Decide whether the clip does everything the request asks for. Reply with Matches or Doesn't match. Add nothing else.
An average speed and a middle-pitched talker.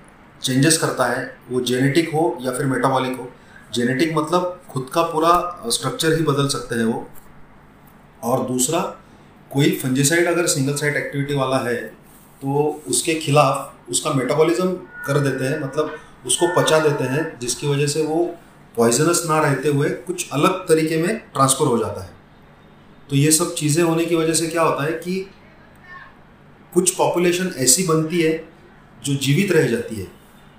Matches